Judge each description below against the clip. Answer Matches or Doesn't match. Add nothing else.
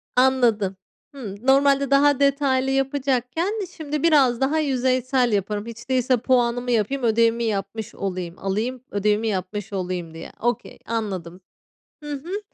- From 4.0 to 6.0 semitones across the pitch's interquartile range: Matches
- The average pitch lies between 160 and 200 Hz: Doesn't match